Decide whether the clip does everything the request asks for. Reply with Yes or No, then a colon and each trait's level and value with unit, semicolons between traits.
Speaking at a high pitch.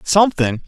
No: medium, 165 Hz